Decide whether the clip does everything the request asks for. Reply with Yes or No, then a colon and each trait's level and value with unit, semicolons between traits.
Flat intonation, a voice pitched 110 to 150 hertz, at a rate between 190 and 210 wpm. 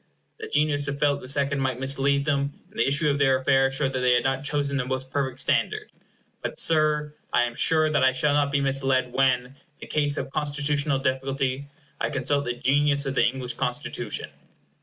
Yes: narrow, 1.6 semitones; medium, 140 Hz; fast, 205 wpm